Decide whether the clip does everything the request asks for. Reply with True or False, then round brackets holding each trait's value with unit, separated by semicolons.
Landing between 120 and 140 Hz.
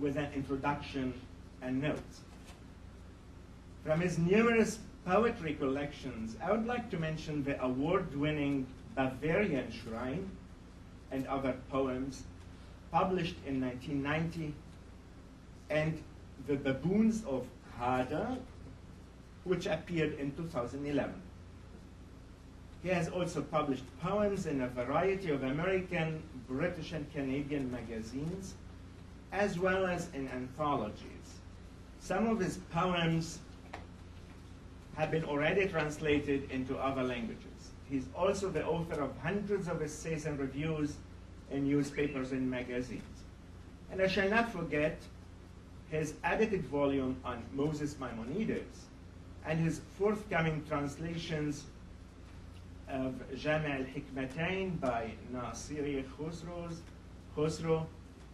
True (135 Hz)